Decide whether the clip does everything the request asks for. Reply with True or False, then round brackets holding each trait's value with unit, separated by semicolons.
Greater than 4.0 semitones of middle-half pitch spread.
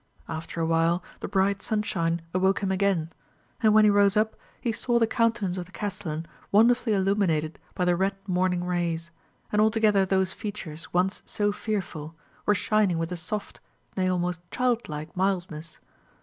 False (3.5 semitones)